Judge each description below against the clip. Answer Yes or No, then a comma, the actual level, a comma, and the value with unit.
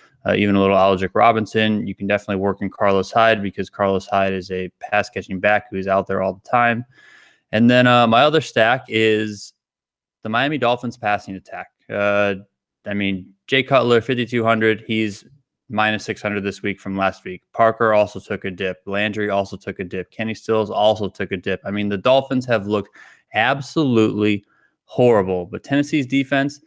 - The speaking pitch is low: Yes, low, 105 Hz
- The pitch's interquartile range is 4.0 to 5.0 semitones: No, average, 3.2 semitones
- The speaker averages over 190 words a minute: No, average, 180 wpm